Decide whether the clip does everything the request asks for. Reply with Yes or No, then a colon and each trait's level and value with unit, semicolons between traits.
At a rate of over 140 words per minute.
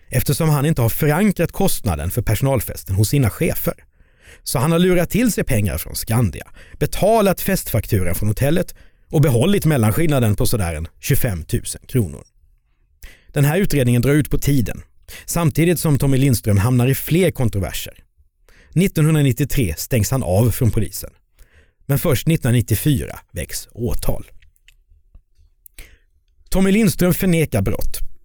No: average, 130 wpm